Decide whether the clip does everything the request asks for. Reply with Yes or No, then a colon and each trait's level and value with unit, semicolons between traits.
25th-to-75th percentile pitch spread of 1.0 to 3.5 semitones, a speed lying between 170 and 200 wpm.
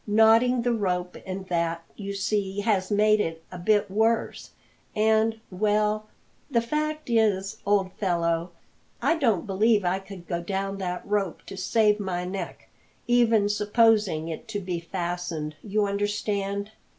No: average, 3.1 semitones; average, 145 wpm